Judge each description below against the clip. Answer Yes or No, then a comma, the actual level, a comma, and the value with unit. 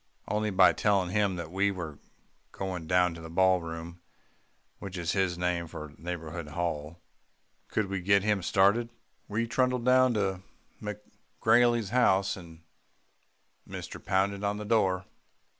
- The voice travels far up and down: No, average, 3.3 semitones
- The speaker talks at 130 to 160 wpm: Yes, average, 140 wpm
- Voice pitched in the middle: No, very low, 95 Hz